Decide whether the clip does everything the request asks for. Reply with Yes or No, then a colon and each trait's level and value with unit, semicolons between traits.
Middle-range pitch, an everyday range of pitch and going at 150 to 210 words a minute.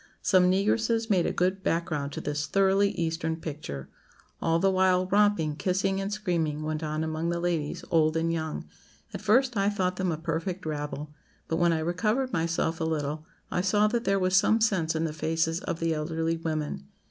Yes: medium, 165 Hz; average, 3.4 semitones; average, 195 wpm